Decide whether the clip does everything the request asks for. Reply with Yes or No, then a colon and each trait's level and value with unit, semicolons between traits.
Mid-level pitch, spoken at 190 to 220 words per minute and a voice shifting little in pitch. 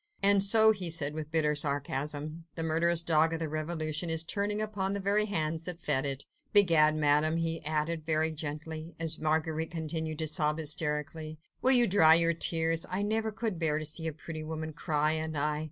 Yes: medium, 160 Hz; average, 195 wpm; narrow, 1.7 semitones